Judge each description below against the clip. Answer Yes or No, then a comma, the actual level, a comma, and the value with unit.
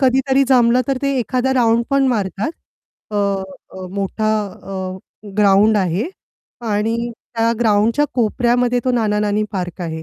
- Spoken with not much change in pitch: No, average, 3.8 semitones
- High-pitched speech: Yes, high, 220 Hz